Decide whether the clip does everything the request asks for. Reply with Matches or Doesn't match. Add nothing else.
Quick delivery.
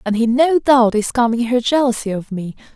Matches